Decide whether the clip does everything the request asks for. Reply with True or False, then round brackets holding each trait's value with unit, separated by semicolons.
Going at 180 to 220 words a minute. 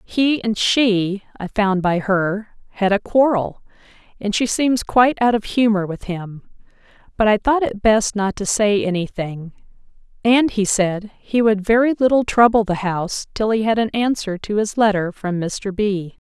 True (185 wpm)